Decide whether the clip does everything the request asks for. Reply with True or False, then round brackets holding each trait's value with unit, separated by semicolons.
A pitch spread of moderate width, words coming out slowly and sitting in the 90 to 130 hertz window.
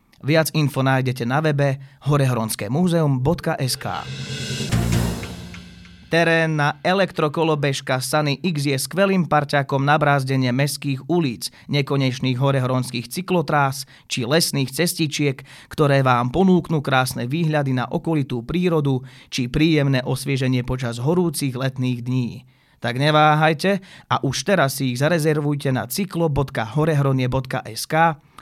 False (3.5 semitones; 105 wpm; 140 Hz)